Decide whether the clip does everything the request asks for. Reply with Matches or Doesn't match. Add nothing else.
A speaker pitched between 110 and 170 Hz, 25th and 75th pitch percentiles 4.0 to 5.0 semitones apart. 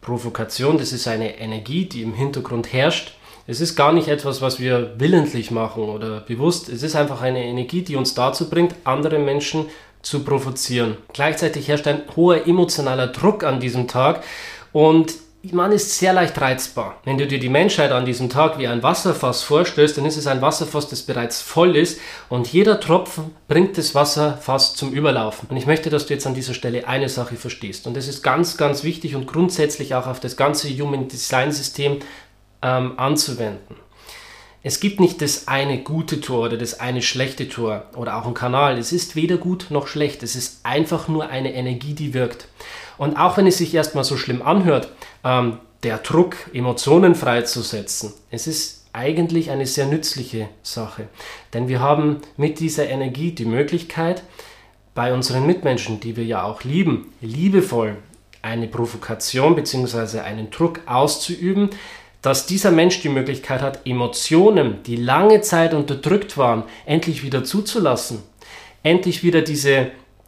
Matches